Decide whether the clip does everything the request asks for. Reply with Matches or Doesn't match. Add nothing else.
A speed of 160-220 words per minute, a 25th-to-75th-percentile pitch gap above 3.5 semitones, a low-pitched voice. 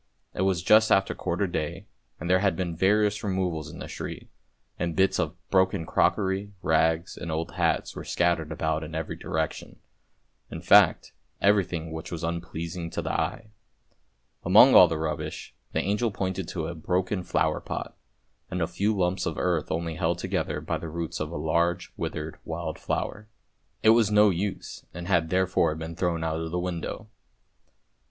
Doesn't match